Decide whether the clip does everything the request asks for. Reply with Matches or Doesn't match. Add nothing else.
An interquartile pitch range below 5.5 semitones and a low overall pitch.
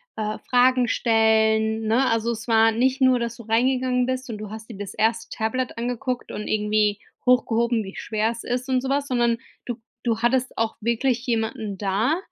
Doesn't match